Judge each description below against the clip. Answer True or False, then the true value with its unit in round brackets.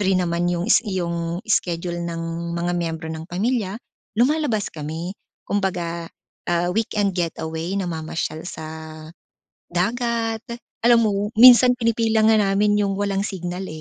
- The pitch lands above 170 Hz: True (185 Hz)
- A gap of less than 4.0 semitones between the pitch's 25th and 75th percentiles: False (4.3 semitones)